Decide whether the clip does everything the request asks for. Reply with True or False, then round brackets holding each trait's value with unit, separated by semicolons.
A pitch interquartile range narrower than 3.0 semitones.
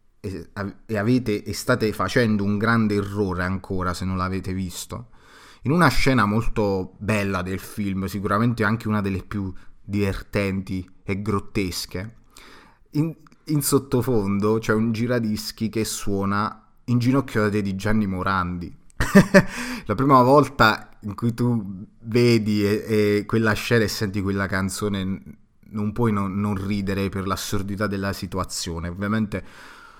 True (2.6 semitones)